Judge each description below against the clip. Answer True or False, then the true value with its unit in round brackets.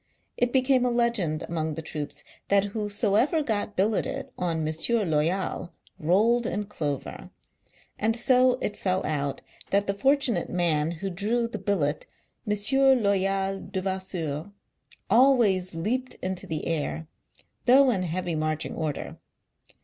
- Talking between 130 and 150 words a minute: True (135 wpm)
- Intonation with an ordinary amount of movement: False (6.0 semitones)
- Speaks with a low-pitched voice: False (195 Hz)